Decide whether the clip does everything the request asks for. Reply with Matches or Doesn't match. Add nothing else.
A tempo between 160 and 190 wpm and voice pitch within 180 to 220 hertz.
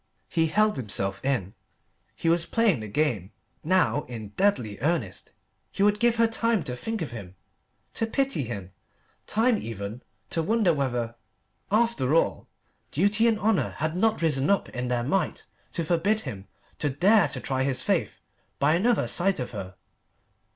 Doesn't match